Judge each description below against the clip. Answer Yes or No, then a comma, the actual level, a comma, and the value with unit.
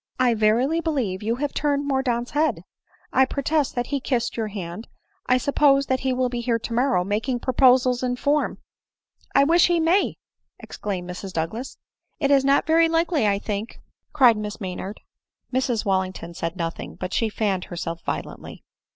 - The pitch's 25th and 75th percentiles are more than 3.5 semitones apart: Yes, average, 5.2 semitones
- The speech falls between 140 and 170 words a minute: No, average, 185 wpm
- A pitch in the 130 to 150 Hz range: No, high, 245 Hz